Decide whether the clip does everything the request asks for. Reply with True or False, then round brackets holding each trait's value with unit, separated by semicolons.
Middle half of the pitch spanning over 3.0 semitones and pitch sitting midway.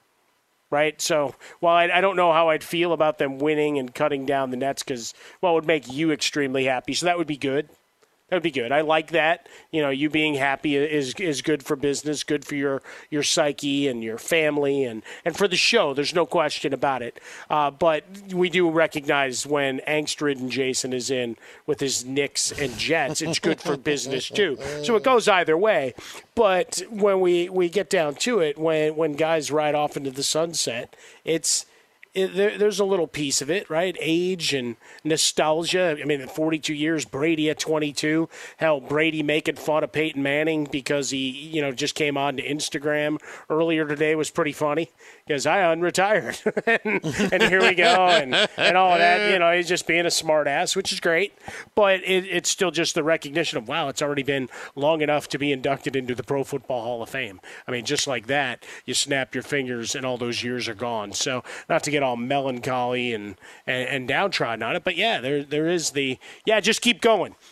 True (3.4 semitones; 150 Hz)